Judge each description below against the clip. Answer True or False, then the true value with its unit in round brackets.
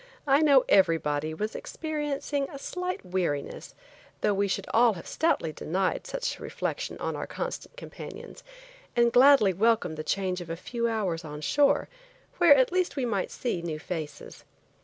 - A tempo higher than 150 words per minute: True (165 wpm)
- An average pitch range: False (8.4 semitones)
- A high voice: True (215 Hz)